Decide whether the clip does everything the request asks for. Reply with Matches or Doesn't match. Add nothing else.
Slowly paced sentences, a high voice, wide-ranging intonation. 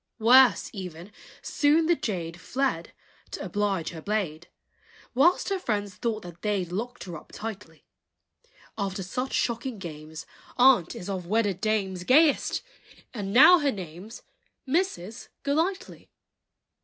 Matches